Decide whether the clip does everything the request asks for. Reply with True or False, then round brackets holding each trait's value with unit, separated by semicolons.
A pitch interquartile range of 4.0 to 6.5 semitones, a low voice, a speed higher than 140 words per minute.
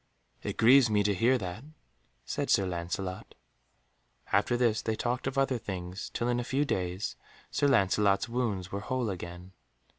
True (4.7 semitones; 105 Hz; 160 wpm)